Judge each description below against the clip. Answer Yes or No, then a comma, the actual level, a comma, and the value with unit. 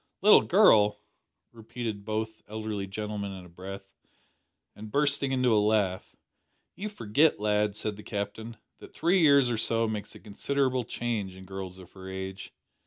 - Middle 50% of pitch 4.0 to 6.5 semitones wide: No, average, 3.2 semitones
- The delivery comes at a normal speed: Yes, average, 160 wpm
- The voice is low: Yes, low, 105 Hz